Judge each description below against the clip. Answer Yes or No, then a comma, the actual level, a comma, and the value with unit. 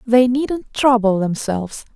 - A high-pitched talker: Yes, high, 235 Hz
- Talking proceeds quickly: No, slow, 125 wpm